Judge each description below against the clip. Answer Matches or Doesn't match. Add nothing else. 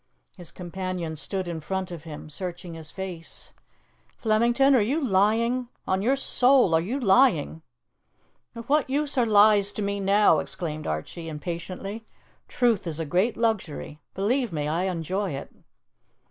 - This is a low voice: Doesn't match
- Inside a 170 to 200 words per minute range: Doesn't match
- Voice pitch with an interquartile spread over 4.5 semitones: Matches